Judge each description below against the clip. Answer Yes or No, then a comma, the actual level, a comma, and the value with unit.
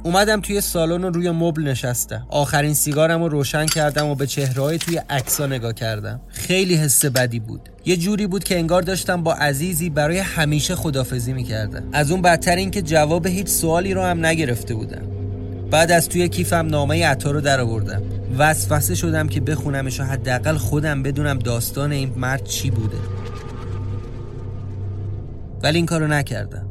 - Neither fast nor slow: No, fast, 160 wpm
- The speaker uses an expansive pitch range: Yes, wide, 6.2 semitones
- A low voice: No, medium, 145 Hz